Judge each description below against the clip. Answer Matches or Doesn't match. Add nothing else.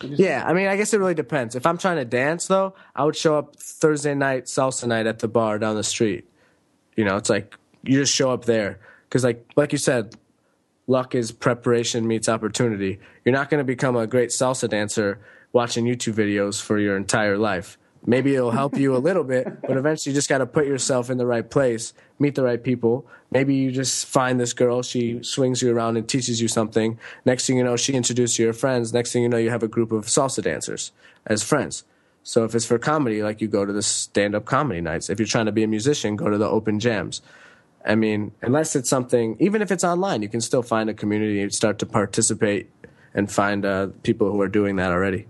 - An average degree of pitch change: Matches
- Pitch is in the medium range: Doesn't match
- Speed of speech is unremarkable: Doesn't match